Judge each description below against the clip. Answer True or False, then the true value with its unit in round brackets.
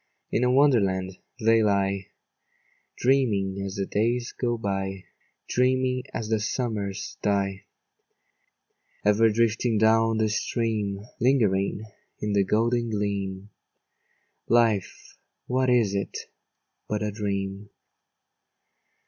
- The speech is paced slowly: True (105 wpm)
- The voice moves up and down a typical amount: True (3.0 semitones)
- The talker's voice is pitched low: True (105 Hz)